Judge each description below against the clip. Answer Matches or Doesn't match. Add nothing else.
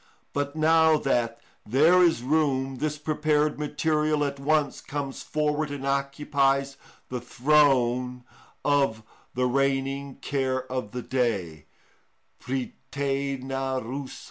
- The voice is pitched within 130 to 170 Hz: Matches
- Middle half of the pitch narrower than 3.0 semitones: Matches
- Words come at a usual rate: Doesn't match